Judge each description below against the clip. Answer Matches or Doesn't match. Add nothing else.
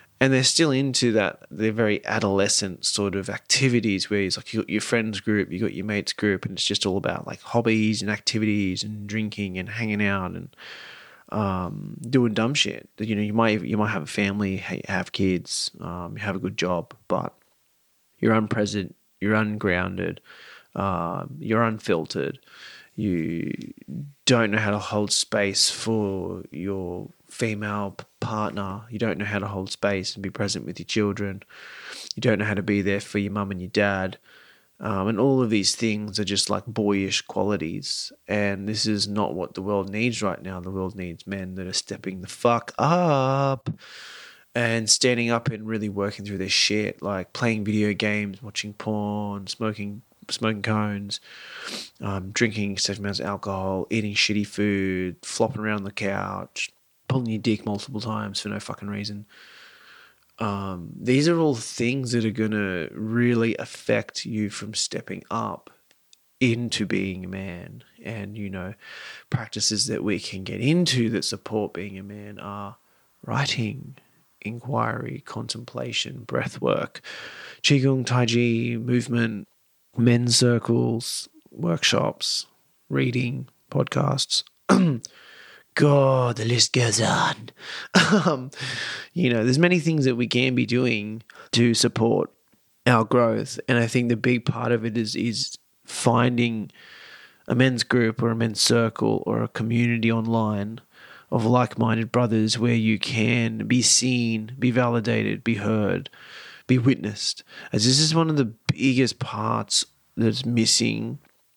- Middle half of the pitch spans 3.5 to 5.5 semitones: Doesn't match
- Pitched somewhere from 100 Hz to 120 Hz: Matches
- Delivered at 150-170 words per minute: Matches